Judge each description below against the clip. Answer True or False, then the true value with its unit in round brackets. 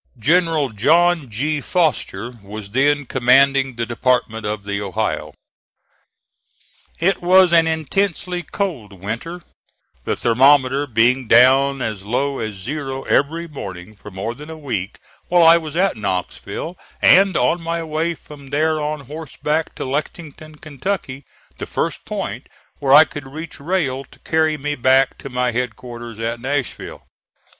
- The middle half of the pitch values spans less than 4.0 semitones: False (5.1 semitones)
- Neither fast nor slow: True (145 wpm)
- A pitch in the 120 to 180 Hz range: True (140 Hz)